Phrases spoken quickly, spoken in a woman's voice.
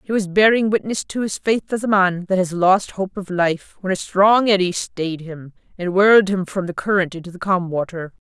Yes: fast, 230 wpm; female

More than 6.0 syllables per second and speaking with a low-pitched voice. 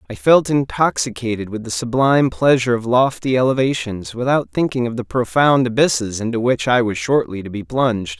No: 5.5 syllables/s; low, 120 Hz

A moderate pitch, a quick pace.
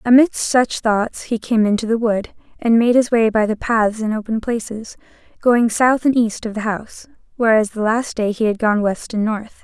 No: high, 225 Hz; fast, 220 wpm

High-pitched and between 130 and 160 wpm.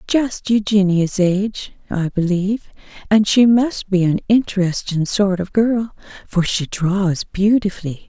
Yes: high, 195 Hz; slow, 135 wpm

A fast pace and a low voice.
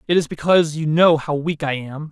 No: fast, 255 wpm; medium, 155 Hz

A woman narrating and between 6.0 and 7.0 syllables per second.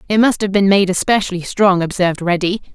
Yes: female; 6.1 syllables/s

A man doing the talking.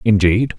Yes: male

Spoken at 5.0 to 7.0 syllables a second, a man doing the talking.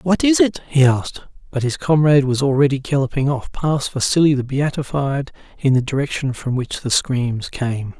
Yes: 5.1 syllables/s; male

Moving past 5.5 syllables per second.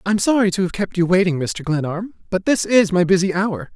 Yes: 5.7 syllables/s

